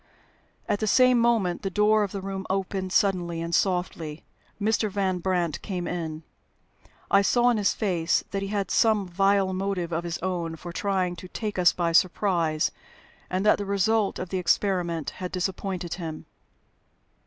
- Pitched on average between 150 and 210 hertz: Yes, medium, 185 Hz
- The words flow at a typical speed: Yes, average, 170 wpm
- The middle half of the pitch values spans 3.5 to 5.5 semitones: No, narrow, 2.5 semitones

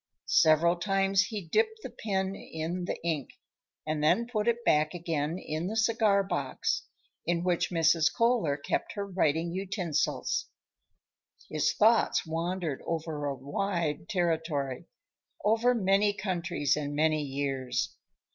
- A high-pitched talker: No, medium, 170 Hz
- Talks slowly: Yes, slow, 130 wpm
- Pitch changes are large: No, average, 4.3 semitones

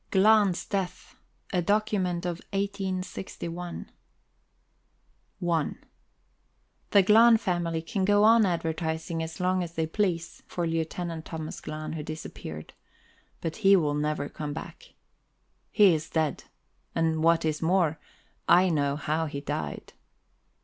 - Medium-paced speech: No, slow, 125 wpm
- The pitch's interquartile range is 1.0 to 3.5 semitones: Yes, average, 3.0 semitones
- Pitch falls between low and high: Yes, medium, 170 Hz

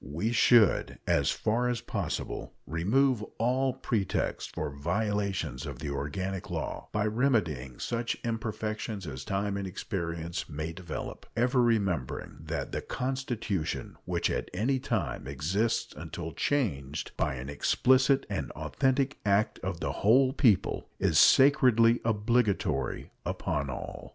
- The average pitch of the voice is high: No, low, 105 Hz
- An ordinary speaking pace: No, slow, 130 wpm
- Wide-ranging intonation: Yes, wide, 6.9 semitones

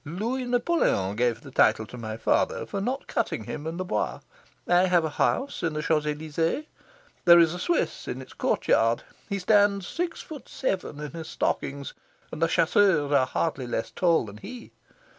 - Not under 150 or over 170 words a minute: No, average, 185 wpm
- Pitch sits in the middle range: Yes, medium, 165 Hz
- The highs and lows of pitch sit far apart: Yes, wide, 6.3 semitones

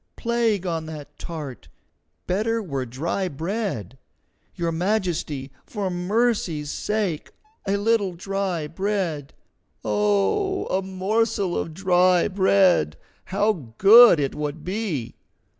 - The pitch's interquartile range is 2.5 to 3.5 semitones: No, average, 4.7 semitones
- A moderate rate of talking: No, slow, 110 wpm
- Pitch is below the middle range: No, medium, 185 Hz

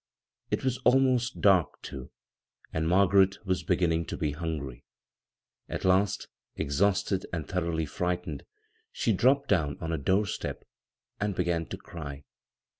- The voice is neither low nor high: No, very low, 90 Hz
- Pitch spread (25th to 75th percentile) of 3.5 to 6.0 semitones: Yes, average, 3.8 semitones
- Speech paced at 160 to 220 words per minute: No, slow, 135 wpm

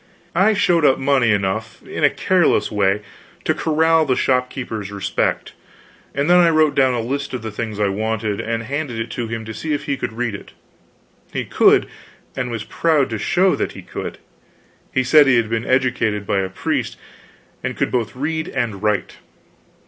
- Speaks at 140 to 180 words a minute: No, average, 190 wpm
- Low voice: Yes, low, 120 Hz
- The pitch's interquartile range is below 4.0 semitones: No, average, 4.6 semitones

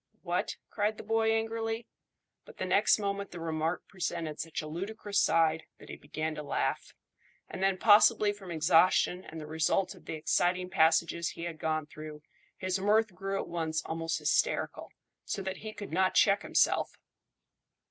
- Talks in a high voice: No, medium, 180 Hz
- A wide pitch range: No, average, 4.1 semitones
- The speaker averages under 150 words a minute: No, average, 170 wpm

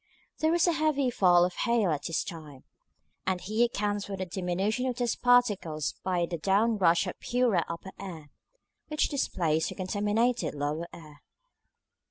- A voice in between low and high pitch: No, high, 195 Hz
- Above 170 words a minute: No, average, 165 wpm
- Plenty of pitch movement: Yes, wide, 5.8 semitones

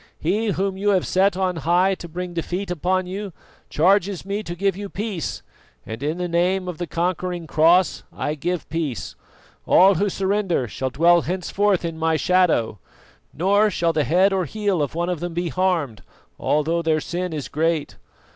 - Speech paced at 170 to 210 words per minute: Yes, average, 185 wpm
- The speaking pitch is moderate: Yes, medium, 175 Hz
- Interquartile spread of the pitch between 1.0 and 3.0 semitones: Yes, average, 2.7 semitones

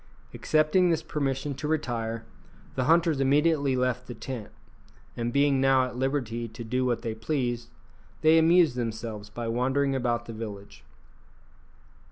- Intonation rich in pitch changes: No, average, 3.8 semitones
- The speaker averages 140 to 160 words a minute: Yes, average, 145 wpm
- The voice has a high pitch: No, low, 130 Hz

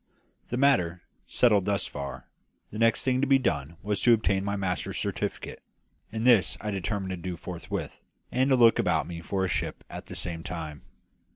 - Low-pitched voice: Yes, low, 100 Hz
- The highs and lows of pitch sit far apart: No, average, 4.8 semitones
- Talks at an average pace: Yes, average, 190 wpm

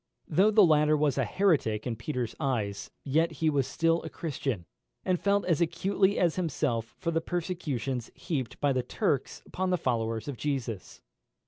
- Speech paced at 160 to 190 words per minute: Yes, average, 175 wpm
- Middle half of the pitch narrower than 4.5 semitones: No, wide, 5.6 semitones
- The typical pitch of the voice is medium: Yes, medium, 150 Hz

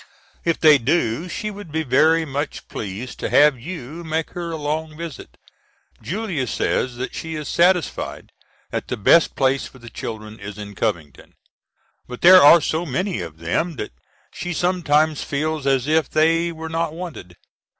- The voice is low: No, medium, 155 Hz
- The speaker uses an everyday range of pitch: Yes, average, 4.9 semitones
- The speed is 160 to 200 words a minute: Yes, average, 170 wpm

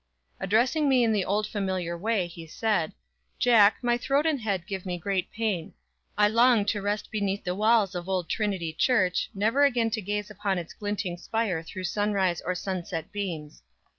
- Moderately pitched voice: No, high, 205 Hz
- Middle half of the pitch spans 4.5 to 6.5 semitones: No, average, 3.4 semitones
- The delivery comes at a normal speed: Yes, average, 180 wpm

